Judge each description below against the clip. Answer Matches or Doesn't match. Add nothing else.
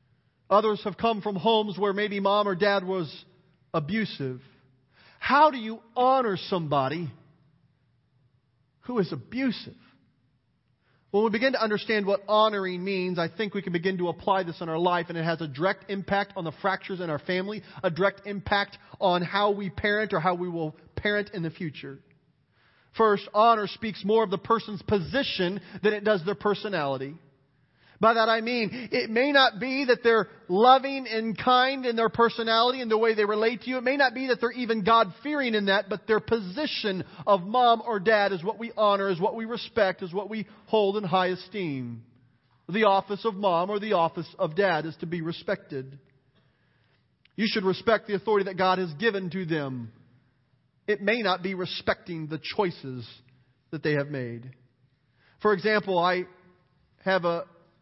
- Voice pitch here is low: Doesn't match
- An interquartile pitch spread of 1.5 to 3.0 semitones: Doesn't match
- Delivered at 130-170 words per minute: Doesn't match